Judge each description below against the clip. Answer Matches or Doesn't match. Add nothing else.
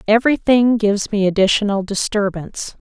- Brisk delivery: Doesn't match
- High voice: Matches